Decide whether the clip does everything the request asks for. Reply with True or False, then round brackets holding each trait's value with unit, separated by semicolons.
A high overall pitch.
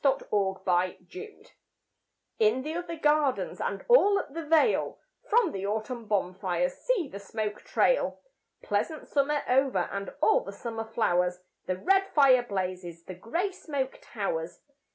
True (245 Hz)